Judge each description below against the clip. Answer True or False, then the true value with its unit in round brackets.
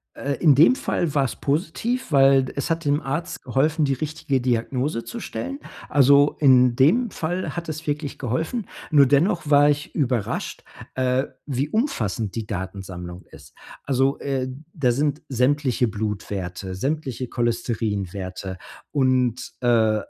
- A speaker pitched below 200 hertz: True (135 Hz)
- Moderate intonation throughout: True (4.2 semitones)